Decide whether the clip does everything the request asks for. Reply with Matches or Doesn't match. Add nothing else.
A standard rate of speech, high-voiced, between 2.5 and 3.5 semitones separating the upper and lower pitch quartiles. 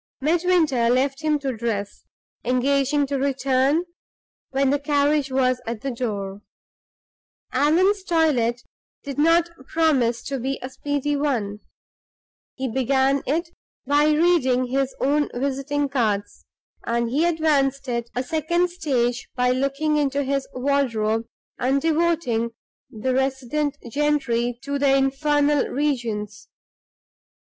Doesn't match